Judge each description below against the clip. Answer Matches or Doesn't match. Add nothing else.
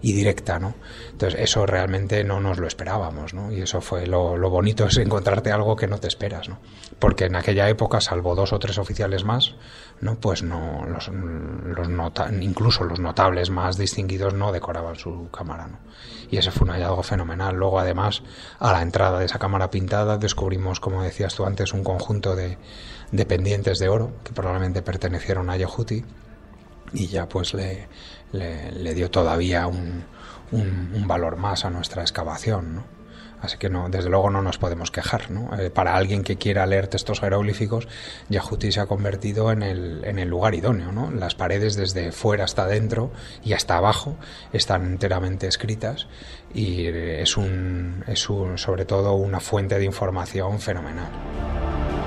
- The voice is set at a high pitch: Doesn't match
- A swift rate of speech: Doesn't match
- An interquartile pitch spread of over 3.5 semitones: Doesn't match